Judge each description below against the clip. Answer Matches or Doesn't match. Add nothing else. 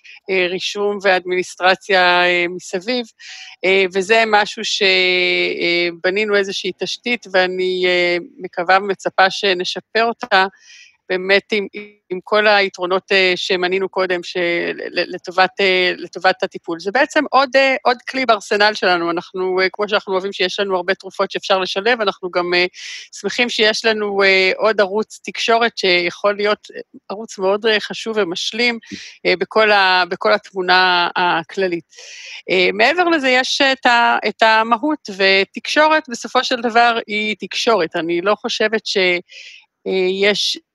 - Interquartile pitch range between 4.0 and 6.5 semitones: Doesn't match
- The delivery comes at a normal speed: Matches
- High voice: Matches